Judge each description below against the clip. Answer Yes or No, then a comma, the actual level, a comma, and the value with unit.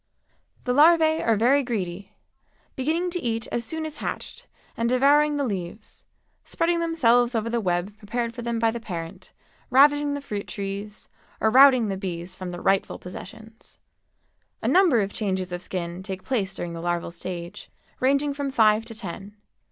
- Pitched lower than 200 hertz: No, high, 225 Hz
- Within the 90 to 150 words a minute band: No, average, 170 wpm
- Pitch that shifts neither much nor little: No, wide, 6.5 semitones